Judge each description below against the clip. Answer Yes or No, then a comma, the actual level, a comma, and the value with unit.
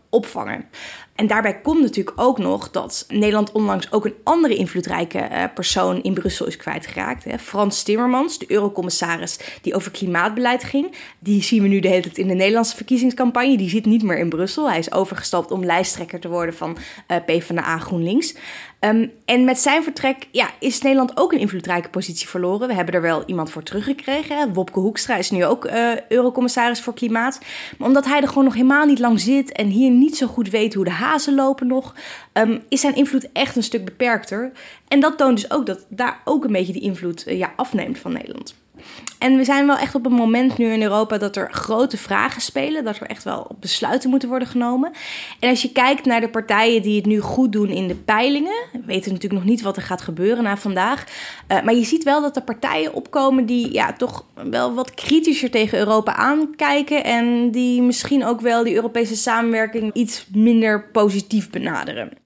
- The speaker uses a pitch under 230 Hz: No, high, 235 Hz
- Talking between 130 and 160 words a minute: No, fast, 200 wpm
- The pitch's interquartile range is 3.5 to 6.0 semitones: Yes, average, 4.6 semitones